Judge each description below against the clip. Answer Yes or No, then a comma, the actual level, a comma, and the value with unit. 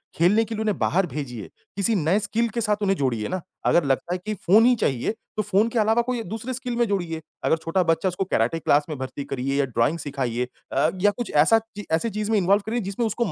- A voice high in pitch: Yes, high, 195 Hz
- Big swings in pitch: Yes, wide, 6.6 semitones